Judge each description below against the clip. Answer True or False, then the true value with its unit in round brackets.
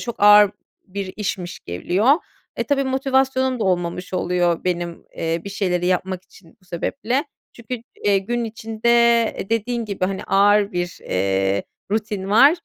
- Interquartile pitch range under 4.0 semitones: False (4.3 semitones)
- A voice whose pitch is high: True (200 Hz)